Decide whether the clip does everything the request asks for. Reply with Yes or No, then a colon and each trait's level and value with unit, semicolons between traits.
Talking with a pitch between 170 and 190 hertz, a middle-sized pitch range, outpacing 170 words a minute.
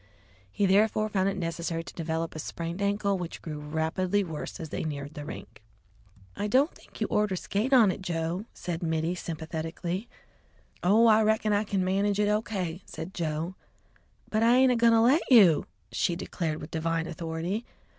Yes: medium, 185 Hz; average, 4.3 semitones; average, 180 wpm